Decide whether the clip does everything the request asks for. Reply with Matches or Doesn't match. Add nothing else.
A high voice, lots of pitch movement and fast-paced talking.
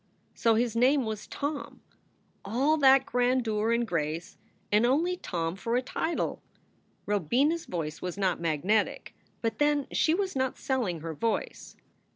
Doesn't match